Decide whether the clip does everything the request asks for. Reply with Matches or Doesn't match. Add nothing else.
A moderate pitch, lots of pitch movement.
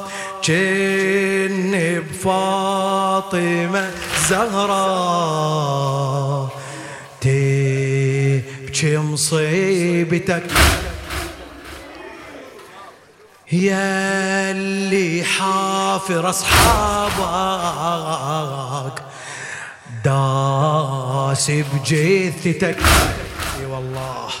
Matches